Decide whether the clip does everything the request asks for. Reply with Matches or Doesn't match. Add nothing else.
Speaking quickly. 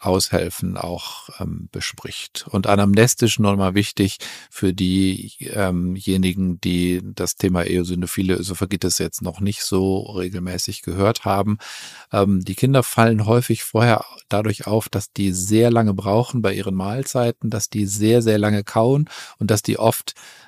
Doesn't match